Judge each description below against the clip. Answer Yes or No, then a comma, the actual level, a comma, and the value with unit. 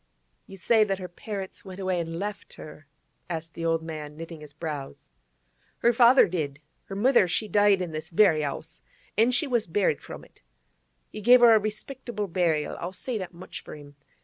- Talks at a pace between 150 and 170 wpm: No, average, 195 wpm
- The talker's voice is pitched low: No, medium, 185 Hz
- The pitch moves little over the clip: No, average, 4.8 semitones